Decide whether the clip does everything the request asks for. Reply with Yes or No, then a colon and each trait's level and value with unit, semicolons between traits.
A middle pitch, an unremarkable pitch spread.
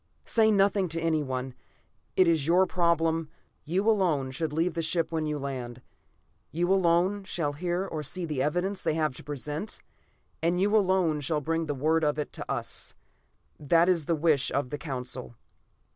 Yes: medium, 165 Hz; average, 3.3 semitones